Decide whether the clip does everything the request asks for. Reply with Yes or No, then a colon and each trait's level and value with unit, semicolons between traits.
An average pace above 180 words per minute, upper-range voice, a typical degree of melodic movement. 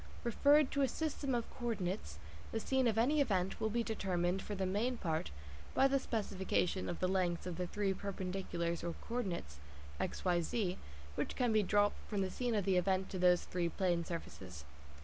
Yes: average, 200 wpm; high, 195 Hz; average, 4.6 semitones